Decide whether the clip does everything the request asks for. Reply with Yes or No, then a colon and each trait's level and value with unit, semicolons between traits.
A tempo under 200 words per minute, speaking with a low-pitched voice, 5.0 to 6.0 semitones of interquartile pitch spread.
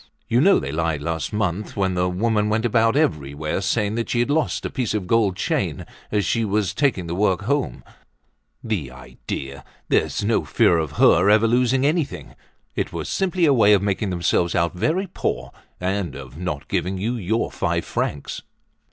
Yes: average, 185 wpm; low, 100 Hz; wide, 5.4 semitones